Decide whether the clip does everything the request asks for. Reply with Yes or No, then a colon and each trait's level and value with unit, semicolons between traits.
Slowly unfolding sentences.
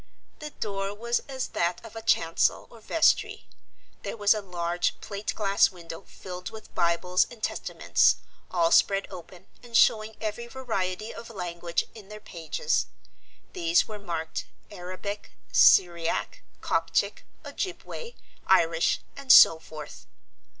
Yes: slow, 130 wpm